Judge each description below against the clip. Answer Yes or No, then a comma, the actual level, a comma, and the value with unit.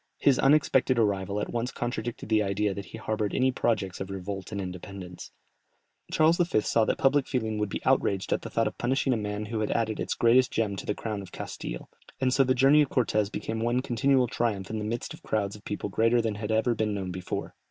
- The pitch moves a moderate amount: Yes, average, 3.6 semitones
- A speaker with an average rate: No, fast, 230 wpm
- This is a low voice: Yes, low, 110 Hz